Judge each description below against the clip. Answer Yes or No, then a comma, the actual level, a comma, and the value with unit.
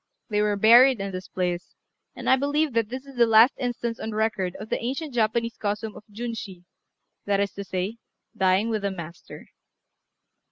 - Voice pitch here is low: No, high, 220 Hz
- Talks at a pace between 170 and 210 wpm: Yes, average, 185 wpm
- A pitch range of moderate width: Yes, average, 3.3 semitones